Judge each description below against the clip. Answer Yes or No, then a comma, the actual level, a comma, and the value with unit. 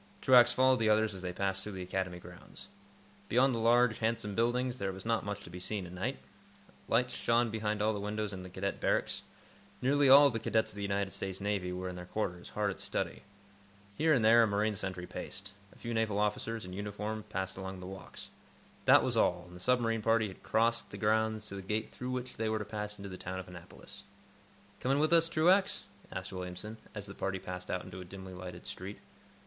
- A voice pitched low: Yes, low, 105 Hz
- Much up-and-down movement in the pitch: No, average, 3.3 semitones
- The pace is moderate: No, fast, 220 wpm